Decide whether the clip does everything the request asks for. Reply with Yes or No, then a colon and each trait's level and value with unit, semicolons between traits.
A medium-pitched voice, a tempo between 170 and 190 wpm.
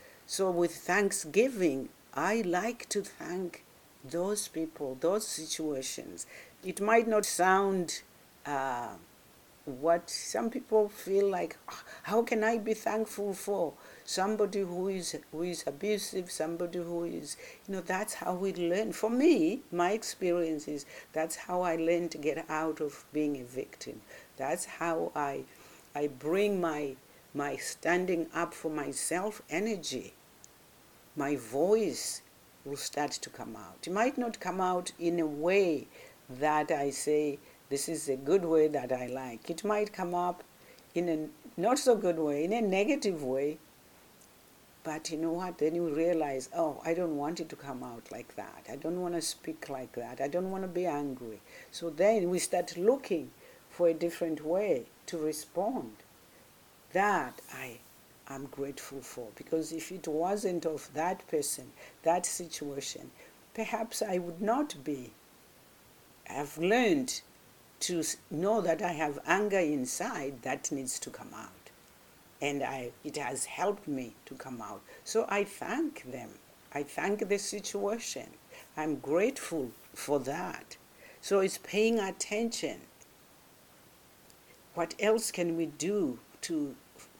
No: medium, 170 Hz; average, 145 wpm